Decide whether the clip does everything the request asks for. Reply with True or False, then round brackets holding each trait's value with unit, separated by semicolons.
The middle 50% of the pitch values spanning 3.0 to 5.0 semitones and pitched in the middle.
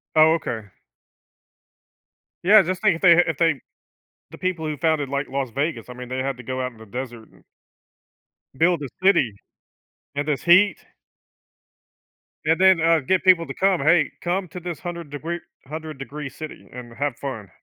True (4.5 semitones; 155 Hz)